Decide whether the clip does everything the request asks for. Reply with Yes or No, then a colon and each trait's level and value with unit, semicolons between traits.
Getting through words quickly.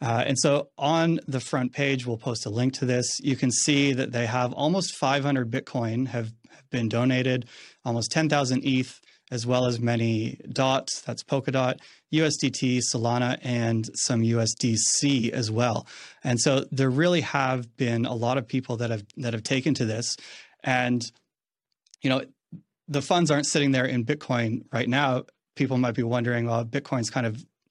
No: average, 170 wpm